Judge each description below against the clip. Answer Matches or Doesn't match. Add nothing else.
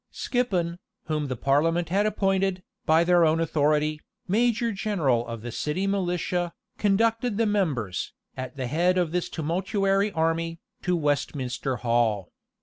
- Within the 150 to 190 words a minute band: Doesn't match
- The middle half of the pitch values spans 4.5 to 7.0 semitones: Matches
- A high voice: Doesn't match